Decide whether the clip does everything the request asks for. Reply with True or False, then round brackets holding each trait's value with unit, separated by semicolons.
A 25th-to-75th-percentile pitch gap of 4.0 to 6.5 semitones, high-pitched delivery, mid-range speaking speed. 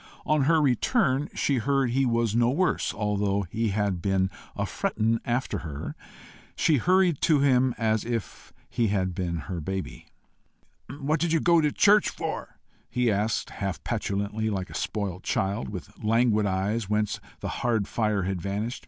False (4.9 semitones; 110 Hz; 165 wpm)